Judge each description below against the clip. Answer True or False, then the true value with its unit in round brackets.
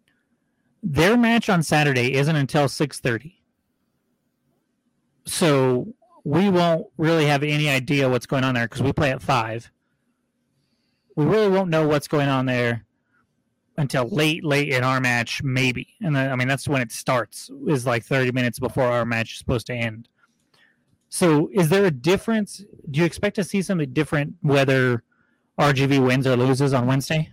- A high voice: False (140 Hz)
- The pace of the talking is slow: False (165 wpm)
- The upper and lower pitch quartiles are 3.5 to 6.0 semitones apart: True (4.0 semitones)